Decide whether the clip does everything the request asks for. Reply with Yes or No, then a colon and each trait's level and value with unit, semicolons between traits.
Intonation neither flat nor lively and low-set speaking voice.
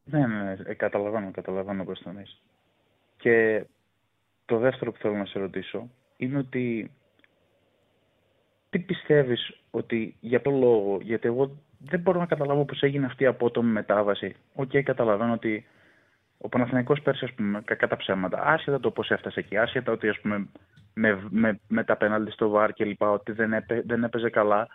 Yes: average, 4.0 semitones; low, 115 Hz